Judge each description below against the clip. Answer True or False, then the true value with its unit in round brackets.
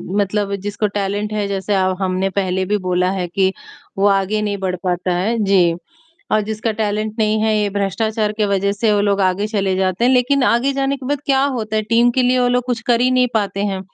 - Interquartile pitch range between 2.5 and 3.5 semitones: True (2.9 semitones)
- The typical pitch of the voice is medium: False (205 Hz)